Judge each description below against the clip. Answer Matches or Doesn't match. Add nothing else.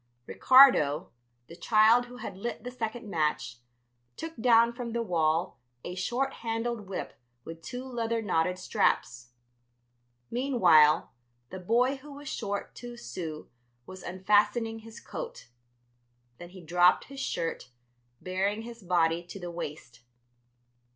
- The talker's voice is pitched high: Matches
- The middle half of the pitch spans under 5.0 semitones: Doesn't match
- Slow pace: Matches